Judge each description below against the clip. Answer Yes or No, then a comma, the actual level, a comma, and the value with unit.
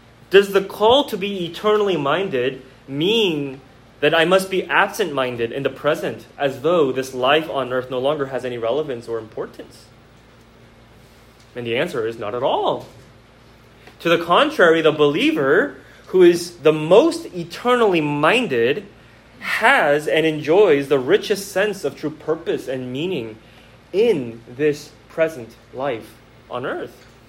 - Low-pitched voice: No, medium, 145 Hz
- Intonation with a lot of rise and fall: Yes, wide, 6.0 semitones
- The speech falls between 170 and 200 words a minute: No, average, 145 wpm